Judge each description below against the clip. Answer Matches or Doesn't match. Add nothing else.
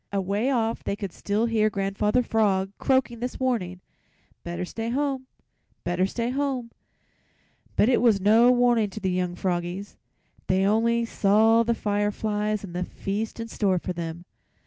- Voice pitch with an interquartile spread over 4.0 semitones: Doesn't match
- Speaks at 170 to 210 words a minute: Doesn't match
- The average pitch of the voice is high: Matches